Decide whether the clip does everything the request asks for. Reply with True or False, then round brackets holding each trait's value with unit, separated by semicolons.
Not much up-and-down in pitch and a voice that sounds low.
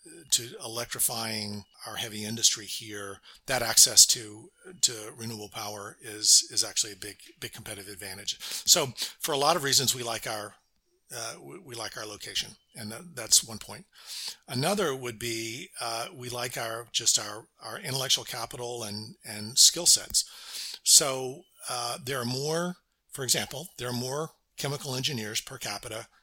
False (3.4 semitones; 115 Hz)